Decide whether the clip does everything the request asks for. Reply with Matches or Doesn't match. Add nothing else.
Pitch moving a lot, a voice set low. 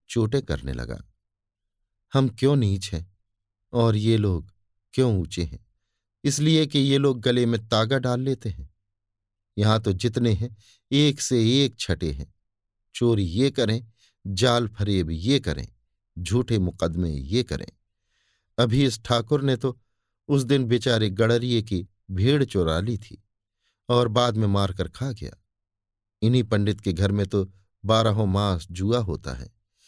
Doesn't match